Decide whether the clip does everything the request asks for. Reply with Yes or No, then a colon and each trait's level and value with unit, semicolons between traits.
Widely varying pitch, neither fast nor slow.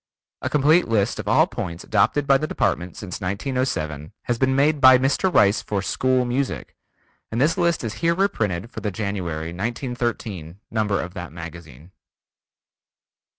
Yes: wide, 6.6 semitones; average, 155 wpm